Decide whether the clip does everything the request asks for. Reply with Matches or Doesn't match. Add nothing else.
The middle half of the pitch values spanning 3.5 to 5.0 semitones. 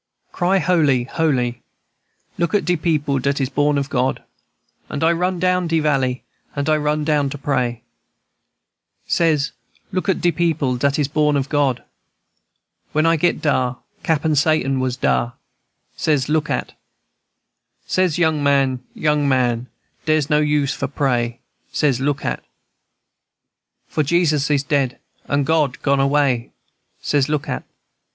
Doesn't match